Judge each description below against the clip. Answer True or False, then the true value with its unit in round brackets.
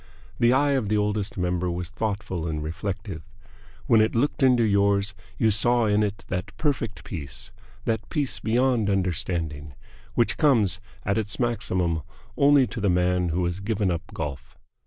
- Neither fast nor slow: True (160 wpm)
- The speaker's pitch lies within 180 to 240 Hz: False (100 Hz)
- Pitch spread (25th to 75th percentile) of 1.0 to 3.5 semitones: False (4.3 semitones)